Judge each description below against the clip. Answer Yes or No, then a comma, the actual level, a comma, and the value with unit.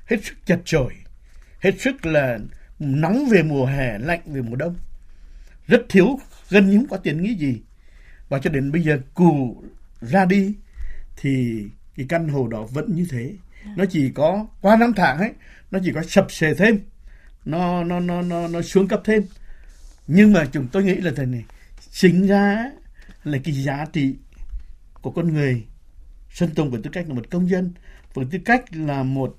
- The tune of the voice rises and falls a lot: Yes, wide, 6.6 semitones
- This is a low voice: No, medium, 160 Hz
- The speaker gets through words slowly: No, average, 190 wpm